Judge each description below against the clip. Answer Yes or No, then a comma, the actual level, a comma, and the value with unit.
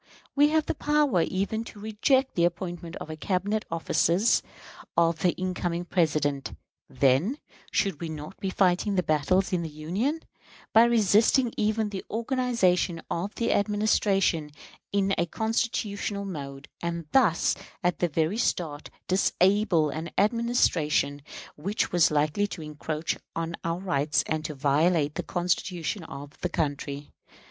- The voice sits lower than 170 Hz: No, medium, 180 Hz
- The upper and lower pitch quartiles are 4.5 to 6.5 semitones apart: Yes, average, 4.9 semitones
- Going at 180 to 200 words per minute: No, average, 140 wpm